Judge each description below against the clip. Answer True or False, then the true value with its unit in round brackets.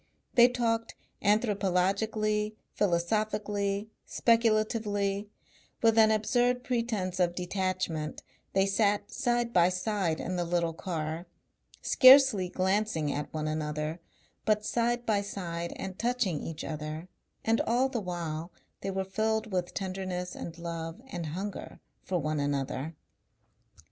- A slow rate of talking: True (125 wpm)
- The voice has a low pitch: False (195 Hz)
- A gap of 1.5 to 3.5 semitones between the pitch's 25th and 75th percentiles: False (4.2 semitones)